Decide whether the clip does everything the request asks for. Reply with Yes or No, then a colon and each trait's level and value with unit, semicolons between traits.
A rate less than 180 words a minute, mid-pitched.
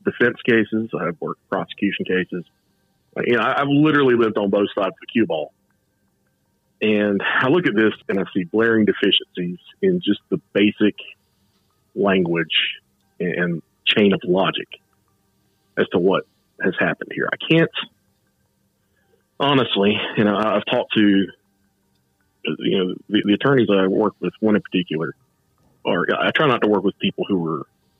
No: average, 160 wpm; low, 100 Hz